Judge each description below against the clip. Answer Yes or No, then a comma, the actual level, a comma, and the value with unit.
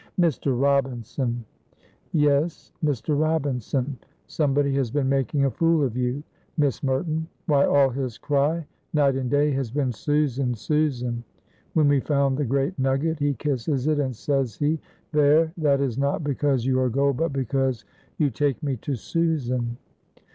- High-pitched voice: No, medium, 140 Hz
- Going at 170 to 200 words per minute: No, average, 155 wpm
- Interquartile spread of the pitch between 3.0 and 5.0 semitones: No, narrow, 2.4 semitones